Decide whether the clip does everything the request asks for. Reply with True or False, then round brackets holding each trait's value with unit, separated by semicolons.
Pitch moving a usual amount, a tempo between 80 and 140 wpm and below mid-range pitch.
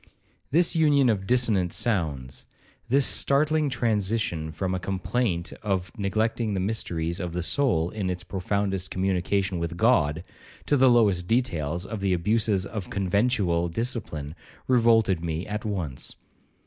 True (4.8 semitones; 135 wpm; 100 Hz)